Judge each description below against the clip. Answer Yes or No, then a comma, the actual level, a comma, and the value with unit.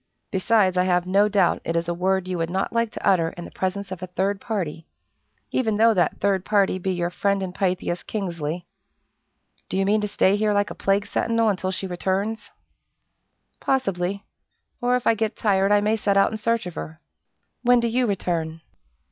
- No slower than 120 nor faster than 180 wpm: No, average, 200 wpm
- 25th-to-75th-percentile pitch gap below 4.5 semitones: Yes, average, 2.8 semitones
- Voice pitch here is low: No, high, 195 Hz